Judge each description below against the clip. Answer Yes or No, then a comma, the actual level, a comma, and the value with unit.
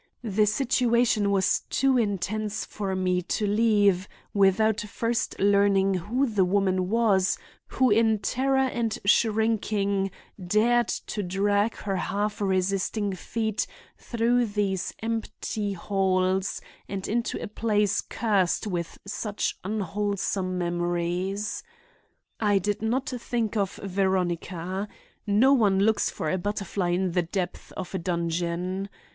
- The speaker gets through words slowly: Yes, slow, 120 wpm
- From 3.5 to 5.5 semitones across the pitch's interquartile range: No, average, 2.7 semitones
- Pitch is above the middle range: Yes, high, 200 Hz